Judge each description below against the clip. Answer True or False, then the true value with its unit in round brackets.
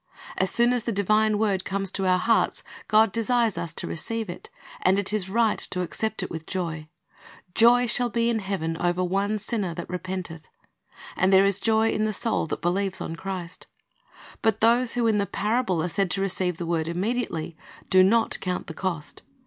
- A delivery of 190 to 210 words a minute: True (200 wpm)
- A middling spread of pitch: True (3.6 semitones)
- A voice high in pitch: True (195 Hz)